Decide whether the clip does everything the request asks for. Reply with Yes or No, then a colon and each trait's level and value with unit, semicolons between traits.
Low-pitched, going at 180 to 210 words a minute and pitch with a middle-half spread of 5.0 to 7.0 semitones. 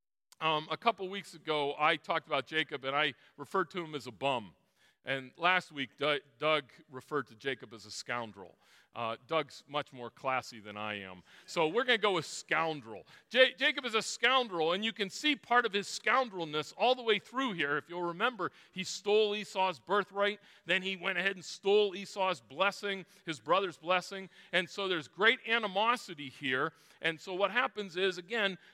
No: medium, 180 Hz; average, 190 wpm; wide, 5.5 semitones